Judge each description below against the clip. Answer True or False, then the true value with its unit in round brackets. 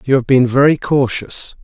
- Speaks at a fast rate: False (185 wpm)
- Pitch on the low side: True (130 Hz)